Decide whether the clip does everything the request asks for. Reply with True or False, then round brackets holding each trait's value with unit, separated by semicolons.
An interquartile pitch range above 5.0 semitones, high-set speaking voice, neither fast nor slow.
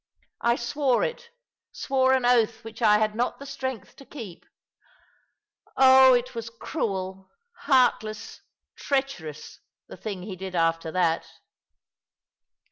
False (5.4 semitones; 230 Hz; 125 wpm)